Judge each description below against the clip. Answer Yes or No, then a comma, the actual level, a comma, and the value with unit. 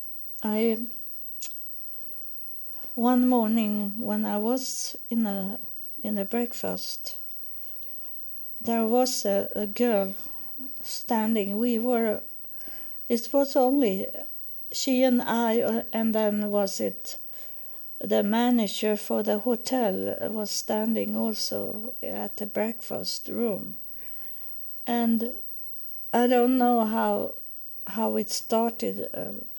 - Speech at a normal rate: No, slow, 105 wpm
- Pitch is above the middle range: Yes, high, 230 Hz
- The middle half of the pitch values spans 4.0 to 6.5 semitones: No, narrow, 2.5 semitones